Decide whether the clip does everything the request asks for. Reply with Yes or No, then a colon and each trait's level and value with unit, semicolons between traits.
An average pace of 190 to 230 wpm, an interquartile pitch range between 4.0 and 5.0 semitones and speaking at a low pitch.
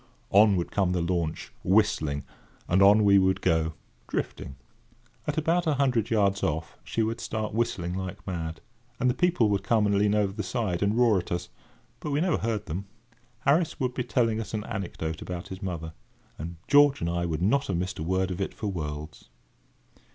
Yes: average, 200 wpm; average, 4.7 semitones; low, 100 Hz